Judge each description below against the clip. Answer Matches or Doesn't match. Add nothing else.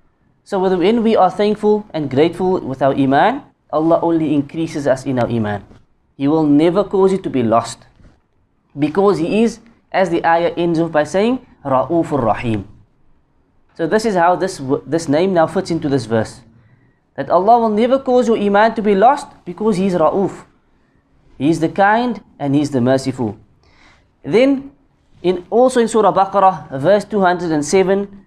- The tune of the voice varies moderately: Doesn't match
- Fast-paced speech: Doesn't match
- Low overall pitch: Doesn't match